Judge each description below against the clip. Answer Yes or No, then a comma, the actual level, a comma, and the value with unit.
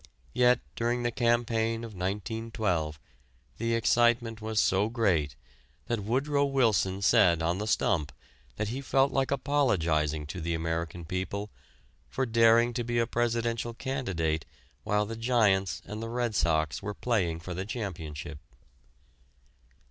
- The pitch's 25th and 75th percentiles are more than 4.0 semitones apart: Yes, average, 5.1 semitones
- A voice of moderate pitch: No, low, 110 Hz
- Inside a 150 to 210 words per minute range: No, slow, 135 wpm